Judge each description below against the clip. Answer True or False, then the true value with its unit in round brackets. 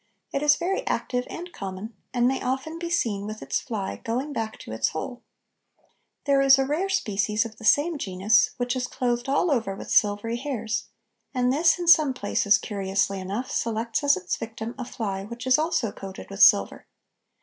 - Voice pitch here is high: True (240 Hz)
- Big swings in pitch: False (5.0 semitones)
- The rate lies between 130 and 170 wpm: False (190 wpm)